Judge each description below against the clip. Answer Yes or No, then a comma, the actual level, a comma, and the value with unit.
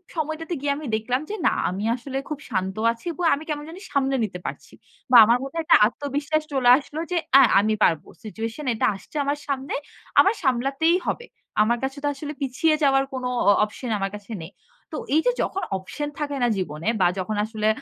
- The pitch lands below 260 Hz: No, very high, 270 Hz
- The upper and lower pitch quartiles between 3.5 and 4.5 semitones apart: No, wide, 5.5 semitones